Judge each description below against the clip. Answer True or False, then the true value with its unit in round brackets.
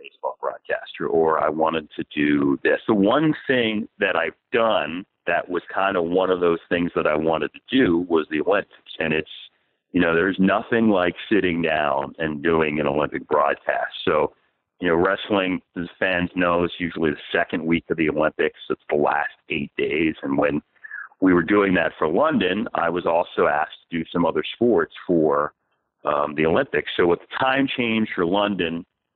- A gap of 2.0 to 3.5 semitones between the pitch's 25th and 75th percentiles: False (4.2 semitones)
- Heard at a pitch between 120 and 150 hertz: False (85 Hz)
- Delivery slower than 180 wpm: False (190 wpm)